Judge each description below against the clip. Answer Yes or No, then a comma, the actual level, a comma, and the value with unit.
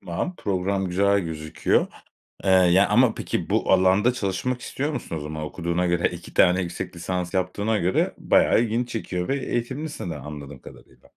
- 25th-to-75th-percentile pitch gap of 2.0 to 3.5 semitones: No, average, 4.5 semitones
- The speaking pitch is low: Yes, very low, 95 Hz